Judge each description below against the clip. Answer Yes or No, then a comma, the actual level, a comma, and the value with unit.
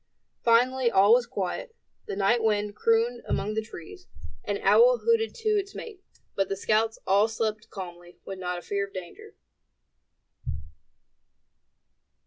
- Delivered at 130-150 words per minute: Yes, average, 140 wpm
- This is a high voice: Yes, high, 220 Hz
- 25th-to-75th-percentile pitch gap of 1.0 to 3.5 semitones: No, average, 4.2 semitones